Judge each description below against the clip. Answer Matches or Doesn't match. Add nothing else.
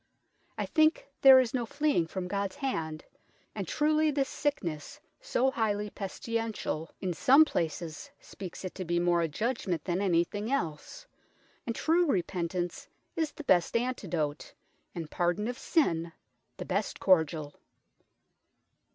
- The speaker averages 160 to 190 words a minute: Doesn't match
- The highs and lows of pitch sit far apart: Matches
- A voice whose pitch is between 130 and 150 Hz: Doesn't match